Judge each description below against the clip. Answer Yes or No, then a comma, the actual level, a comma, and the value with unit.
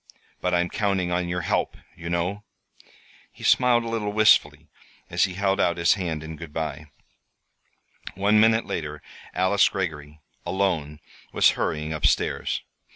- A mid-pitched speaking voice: No, very low, 90 Hz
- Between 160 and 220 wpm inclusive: No, average, 150 wpm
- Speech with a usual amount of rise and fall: Yes, average, 4.1 semitones